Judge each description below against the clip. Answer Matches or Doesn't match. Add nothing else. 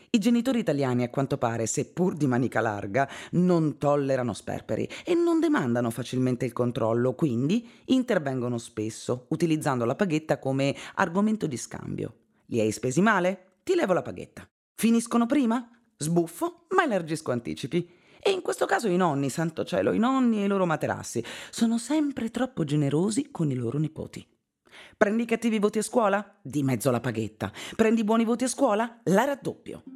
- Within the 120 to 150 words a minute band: Doesn't match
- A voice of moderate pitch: Matches